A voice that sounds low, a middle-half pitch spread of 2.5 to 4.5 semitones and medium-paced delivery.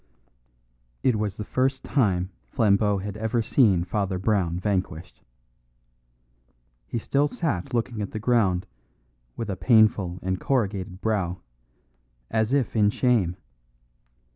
No: low, 105 Hz; average, 3.7 semitones; slow, 120 wpm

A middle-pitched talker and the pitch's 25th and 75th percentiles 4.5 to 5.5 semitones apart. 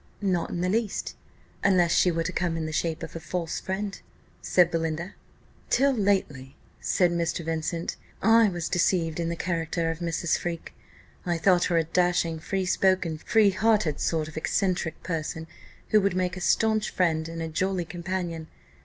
No: medium, 175 Hz; narrow, 2.4 semitones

